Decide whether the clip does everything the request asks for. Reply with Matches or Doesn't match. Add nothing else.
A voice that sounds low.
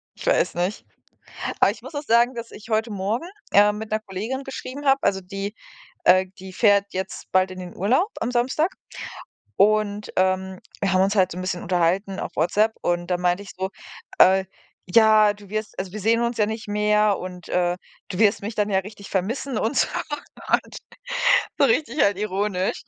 Doesn't match